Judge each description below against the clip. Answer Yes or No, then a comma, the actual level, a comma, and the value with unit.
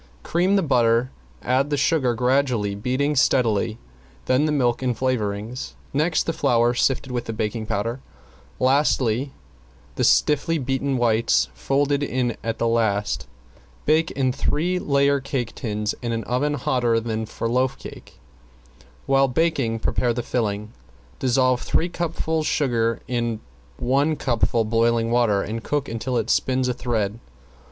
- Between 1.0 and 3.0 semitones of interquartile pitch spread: No, average, 3.4 semitones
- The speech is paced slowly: No, average, 145 wpm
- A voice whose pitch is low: Yes, low, 125 Hz